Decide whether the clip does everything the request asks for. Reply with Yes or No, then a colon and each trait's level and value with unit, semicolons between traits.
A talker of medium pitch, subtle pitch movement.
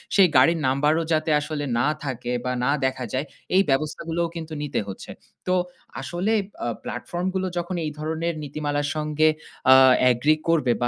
No: medium, 155 Hz; average, 3.7 semitones